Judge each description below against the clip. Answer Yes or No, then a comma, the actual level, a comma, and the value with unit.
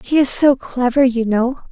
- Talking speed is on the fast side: Yes, fast, 210 wpm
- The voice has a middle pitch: No, very high, 255 Hz